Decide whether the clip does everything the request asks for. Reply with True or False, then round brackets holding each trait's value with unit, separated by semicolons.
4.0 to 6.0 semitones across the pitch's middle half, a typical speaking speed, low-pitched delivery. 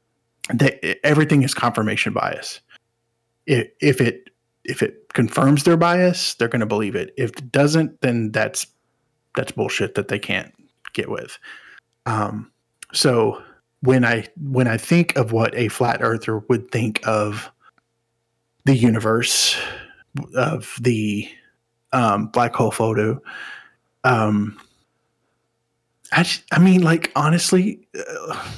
False (5.5 semitones; 130 wpm; 120 Hz)